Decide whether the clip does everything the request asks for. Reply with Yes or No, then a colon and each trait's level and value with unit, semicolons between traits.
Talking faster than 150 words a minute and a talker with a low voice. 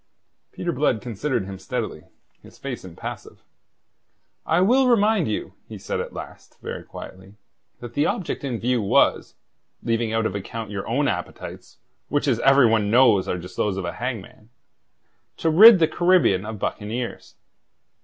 Yes: average, 160 wpm; low, 115 Hz